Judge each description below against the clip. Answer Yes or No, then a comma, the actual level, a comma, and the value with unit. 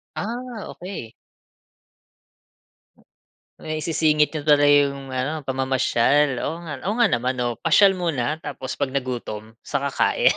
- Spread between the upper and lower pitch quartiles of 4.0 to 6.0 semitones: No, average, 3.5 semitones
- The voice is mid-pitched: Yes, medium, 145 Hz